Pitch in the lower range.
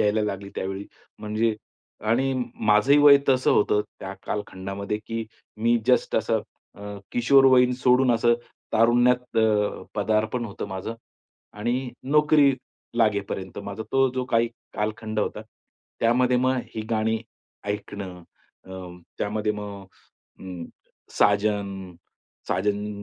Yes: low, 110 Hz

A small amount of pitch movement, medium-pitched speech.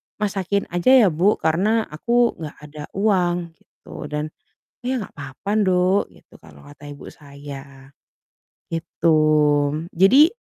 No: average, 5.2 semitones; medium, 170 Hz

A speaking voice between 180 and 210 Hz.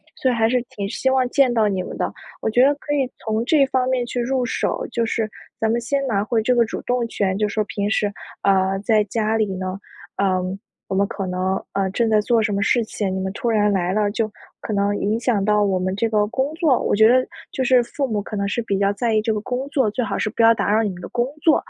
No: high, 220 Hz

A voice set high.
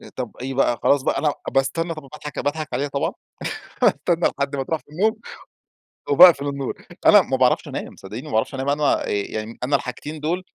No: medium, 140 Hz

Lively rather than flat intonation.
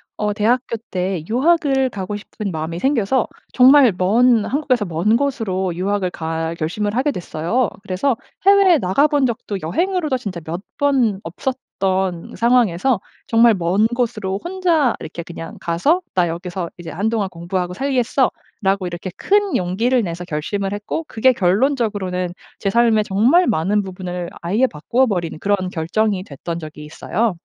Yes: wide, 5.9 semitones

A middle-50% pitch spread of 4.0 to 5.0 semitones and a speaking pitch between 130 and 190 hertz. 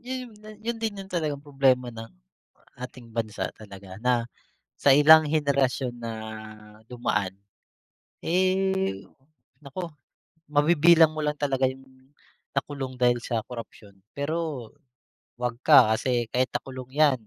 Yes: average, 4.5 semitones; low, 135 Hz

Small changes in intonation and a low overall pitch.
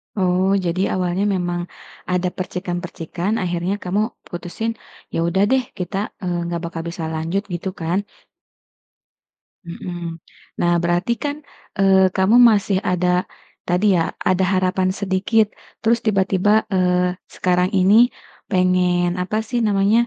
No: narrow, 2.0 semitones; medium, 185 Hz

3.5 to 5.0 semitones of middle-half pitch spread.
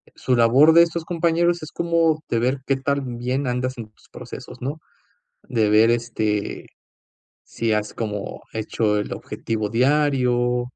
Yes: average, 4.7 semitones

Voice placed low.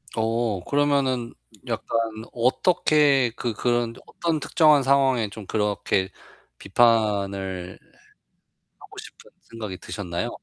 Yes: low, 115 Hz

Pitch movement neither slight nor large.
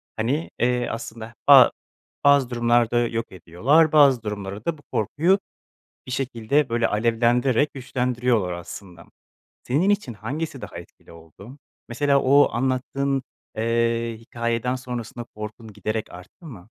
Yes: average, 3.6 semitones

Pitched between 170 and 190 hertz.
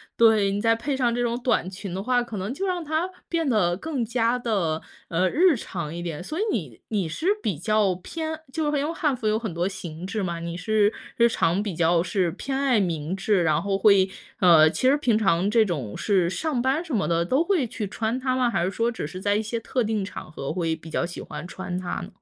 No: high, 210 Hz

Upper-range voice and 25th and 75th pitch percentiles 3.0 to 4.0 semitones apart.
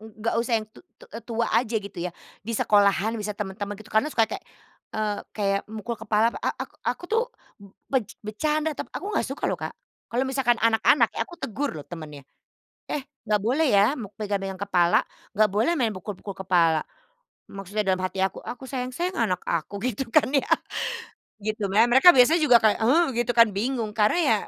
Yes: high, 220 Hz; average, 3.7 semitones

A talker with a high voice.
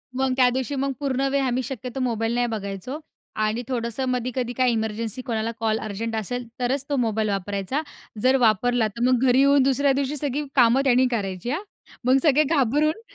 Yes: high, 245 Hz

